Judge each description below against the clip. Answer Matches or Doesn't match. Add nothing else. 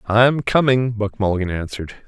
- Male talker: Matches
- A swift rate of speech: Doesn't match